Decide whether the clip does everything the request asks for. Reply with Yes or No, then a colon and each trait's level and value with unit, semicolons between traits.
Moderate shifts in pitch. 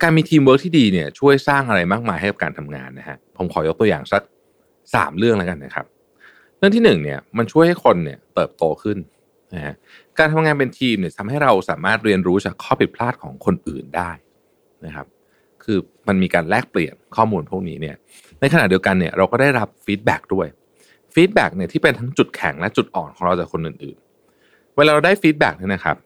No: wide, 8.7 semitones